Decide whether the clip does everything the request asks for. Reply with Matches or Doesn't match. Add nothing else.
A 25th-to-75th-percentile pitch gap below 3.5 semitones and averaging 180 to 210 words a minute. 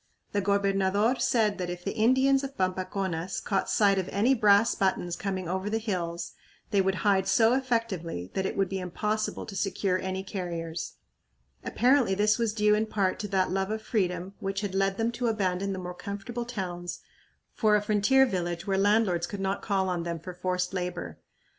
Matches